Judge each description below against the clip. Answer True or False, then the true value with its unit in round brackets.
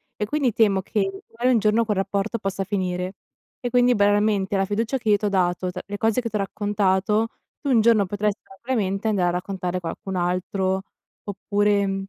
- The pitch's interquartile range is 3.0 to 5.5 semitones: False (2.4 semitones)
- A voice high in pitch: True (205 Hz)